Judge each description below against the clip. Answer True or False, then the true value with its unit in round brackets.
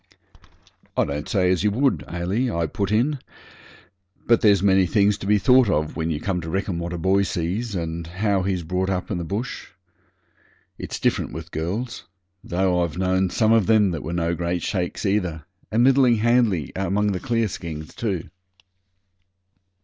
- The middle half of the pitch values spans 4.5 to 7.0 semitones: False (3.7 semitones)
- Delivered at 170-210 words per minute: True (175 wpm)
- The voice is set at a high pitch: False (95 Hz)